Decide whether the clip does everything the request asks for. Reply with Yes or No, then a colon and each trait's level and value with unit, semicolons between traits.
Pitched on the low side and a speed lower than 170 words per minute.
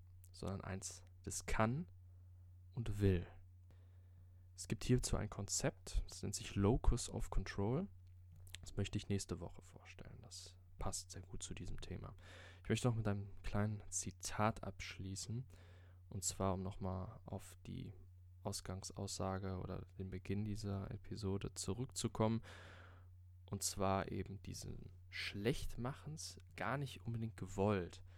Yes: very low, 95 Hz; average, 130 wpm